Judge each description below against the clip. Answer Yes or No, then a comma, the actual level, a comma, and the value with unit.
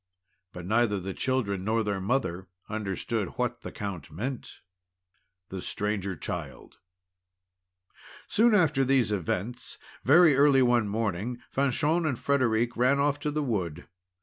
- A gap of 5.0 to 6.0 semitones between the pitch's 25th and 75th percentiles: Yes, average, 5.3 semitones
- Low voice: Yes, low, 120 Hz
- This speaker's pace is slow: Yes, slow, 130 wpm